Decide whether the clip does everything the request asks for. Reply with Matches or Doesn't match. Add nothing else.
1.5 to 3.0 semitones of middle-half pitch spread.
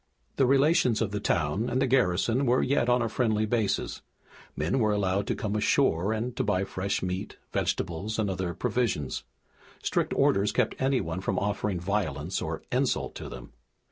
Doesn't match